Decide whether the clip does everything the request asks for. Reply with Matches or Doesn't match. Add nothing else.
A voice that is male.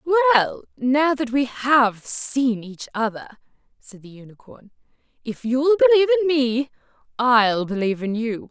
Doesn't match